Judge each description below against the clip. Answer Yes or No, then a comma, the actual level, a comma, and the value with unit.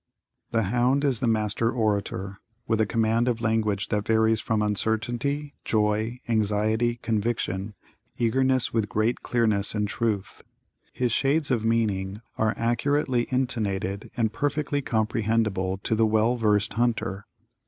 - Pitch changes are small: Yes, narrow, 2.2 semitones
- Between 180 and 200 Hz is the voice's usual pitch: No, low, 110 Hz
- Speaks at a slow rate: Yes, slow, 130 wpm